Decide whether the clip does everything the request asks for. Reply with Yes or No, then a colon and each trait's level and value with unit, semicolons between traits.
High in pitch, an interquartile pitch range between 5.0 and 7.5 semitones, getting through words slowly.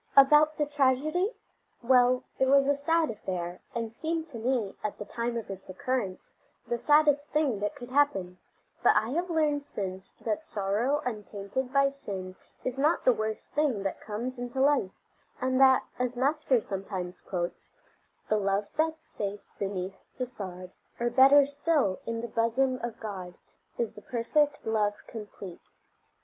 No: high, 245 Hz; wide, 5.6 semitones; average, 160 wpm